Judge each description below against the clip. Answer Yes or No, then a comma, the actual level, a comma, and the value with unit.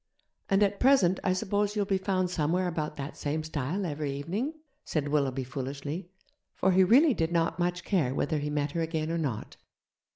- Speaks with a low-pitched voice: No, medium, 165 Hz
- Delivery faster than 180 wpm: Yes, average, 190 wpm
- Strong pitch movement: No, average, 4.5 semitones